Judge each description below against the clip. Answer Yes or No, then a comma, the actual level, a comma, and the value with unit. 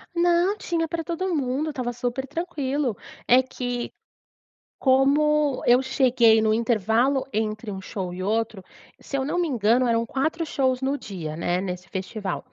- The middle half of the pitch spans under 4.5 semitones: No, average, 4.8 semitones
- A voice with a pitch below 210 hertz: No, very high, 255 Hz